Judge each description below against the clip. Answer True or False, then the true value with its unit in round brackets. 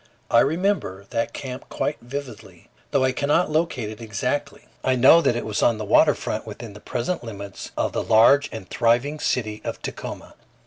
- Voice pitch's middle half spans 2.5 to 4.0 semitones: False (4.6 semitones)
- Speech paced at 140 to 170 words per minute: False (185 wpm)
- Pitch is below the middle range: True (120 Hz)